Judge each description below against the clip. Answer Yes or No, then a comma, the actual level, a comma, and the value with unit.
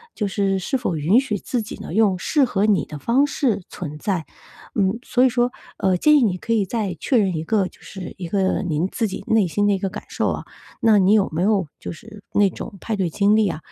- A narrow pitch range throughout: No, average, 3.3 semitones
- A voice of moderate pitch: No, high, 200 Hz